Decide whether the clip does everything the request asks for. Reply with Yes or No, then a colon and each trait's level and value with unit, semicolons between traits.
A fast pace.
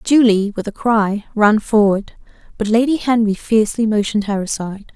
No: average, 155 wpm